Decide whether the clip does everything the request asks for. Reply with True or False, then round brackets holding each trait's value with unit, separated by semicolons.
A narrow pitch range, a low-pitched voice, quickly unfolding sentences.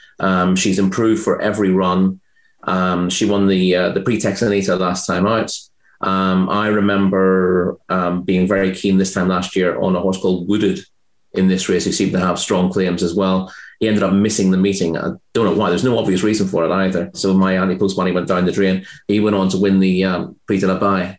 True (1.2 semitones; 95 Hz; 220 wpm)